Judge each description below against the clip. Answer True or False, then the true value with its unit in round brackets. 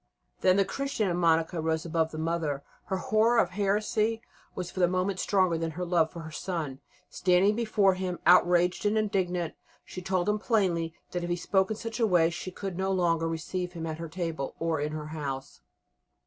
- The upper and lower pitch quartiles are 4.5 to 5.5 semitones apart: False (2.9 semitones)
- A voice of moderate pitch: True (180 Hz)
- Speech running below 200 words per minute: False (205 wpm)